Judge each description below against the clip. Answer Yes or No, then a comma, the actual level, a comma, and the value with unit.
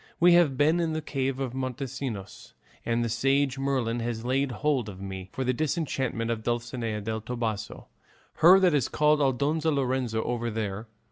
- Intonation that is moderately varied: Yes, average, 3.6 semitones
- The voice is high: No, low, 130 Hz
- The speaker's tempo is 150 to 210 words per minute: Yes, average, 175 wpm